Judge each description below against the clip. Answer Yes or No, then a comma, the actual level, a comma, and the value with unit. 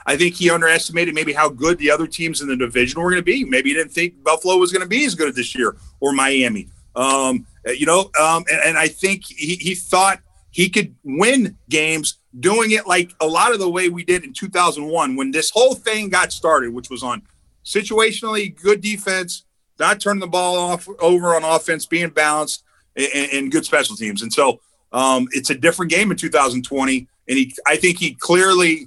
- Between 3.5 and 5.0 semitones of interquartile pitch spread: Yes, average, 4.2 semitones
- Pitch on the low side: No, medium, 170 Hz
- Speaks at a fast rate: Yes, fast, 210 wpm